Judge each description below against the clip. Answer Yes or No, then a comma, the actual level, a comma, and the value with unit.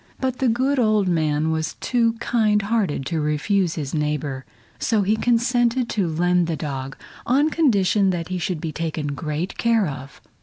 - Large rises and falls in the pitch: Yes, wide, 6.9 semitones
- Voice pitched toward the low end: No, medium, 185 Hz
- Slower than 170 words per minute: No, average, 175 wpm